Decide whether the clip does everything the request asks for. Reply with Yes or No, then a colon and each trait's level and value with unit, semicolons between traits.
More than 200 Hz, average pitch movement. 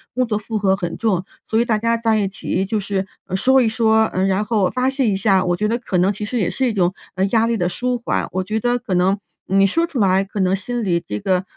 Yes: high, 210 Hz; average, 3.6 semitones